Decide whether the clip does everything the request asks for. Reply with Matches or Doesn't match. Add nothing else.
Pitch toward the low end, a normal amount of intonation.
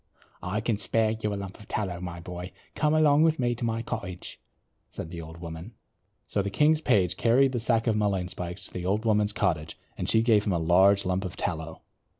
Matches